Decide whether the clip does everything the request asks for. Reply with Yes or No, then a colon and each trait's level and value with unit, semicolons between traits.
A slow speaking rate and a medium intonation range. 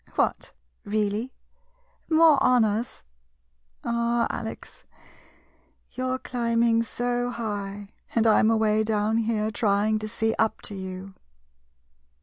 No: slow, 115 wpm; narrow, 2.0 semitones